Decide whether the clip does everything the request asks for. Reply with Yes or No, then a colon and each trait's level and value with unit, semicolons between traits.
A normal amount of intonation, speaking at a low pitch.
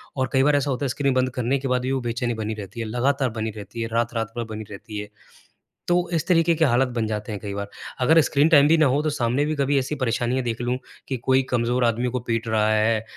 Yes: average, 3.5 semitones; low, 125 Hz